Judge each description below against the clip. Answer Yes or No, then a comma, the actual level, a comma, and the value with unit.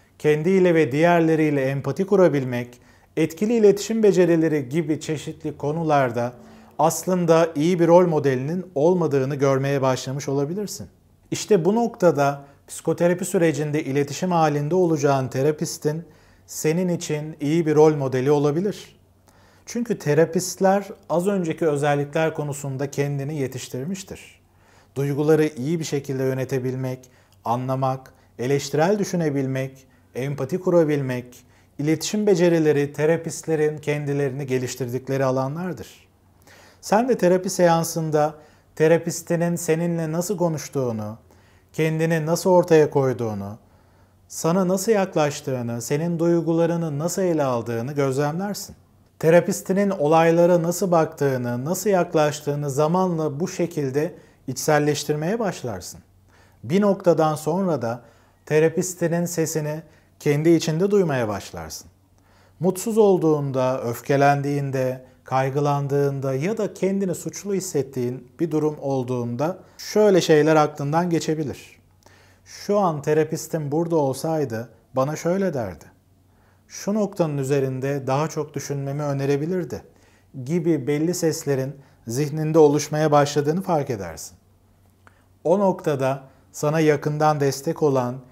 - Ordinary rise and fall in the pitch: Yes, average, 4.5 semitones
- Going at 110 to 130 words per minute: No, average, 100 wpm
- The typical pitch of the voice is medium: Yes, medium, 150 Hz